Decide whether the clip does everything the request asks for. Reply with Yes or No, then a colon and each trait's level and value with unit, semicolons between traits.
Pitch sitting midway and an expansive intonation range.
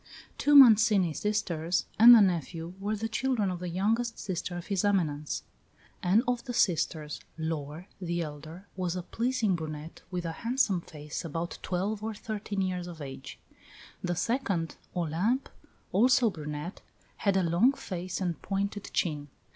No: medium, 180 Hz; average, 4.5 semitones